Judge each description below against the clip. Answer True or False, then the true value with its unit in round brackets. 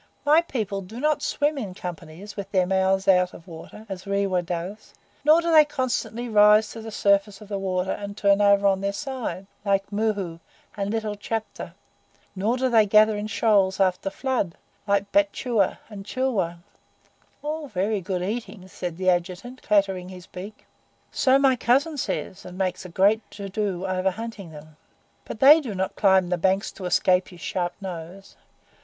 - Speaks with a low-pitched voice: False (200 Hz)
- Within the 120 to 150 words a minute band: False (180 wpm)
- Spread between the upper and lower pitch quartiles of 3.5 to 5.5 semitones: False (3.1 semitones)